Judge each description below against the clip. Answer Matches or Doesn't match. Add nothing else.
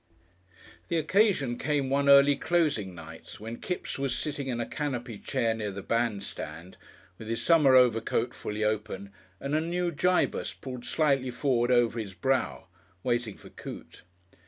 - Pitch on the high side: Doesn't match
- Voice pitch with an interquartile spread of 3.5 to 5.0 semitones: Matches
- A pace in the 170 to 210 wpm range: Doesn't match